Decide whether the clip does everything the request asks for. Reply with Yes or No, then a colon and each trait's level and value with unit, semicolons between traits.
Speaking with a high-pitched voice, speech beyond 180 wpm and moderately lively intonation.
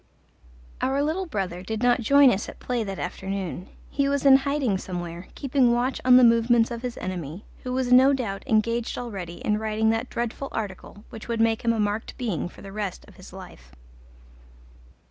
Yes: high, 225 Hz; average, 190 wpm; average, 4.4 semitones